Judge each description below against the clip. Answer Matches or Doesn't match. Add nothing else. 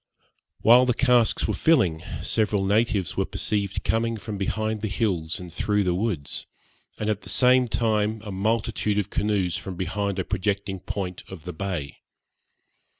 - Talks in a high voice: Doesn't match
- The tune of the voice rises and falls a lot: Doesn't match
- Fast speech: Doesn't match